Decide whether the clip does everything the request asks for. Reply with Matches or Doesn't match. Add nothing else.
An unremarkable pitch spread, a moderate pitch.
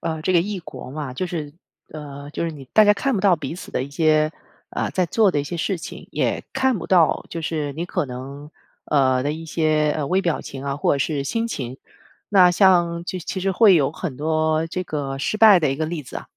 Matches